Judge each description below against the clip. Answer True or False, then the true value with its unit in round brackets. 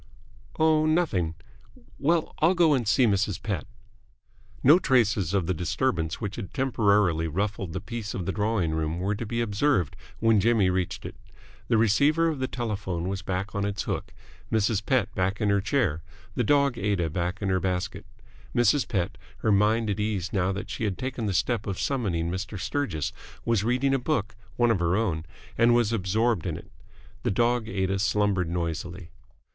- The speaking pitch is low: True (105 Hz)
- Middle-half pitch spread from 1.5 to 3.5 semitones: False (4.3 semitones)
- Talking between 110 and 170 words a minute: False (185 wpm)